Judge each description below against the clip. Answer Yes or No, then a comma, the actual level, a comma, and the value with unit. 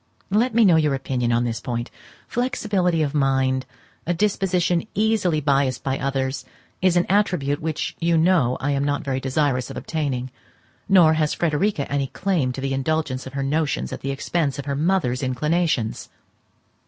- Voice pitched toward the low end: No, medium, 145 Hz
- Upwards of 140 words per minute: Yes, average, 170 wpm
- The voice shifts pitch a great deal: No, average, 4.6 semitones